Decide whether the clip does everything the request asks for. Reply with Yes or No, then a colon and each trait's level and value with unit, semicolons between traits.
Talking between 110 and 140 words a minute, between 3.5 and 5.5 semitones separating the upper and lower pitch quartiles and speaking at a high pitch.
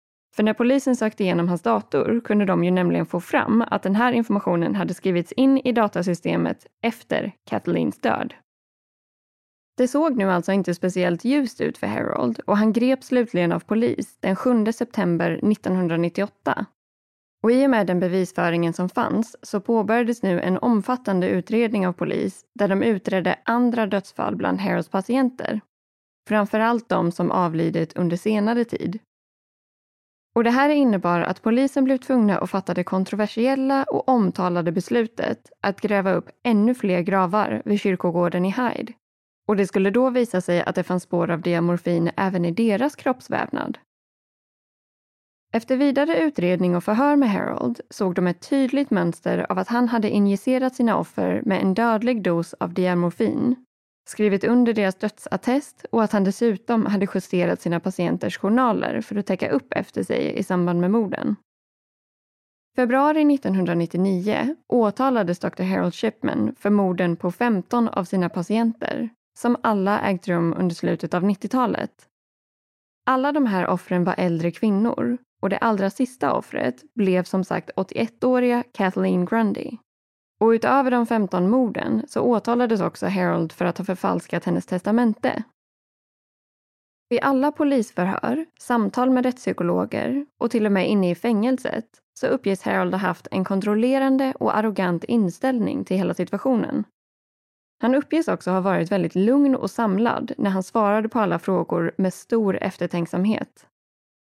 No: average, 150 wpm; average, 4.8 semitones; high, 210 Hz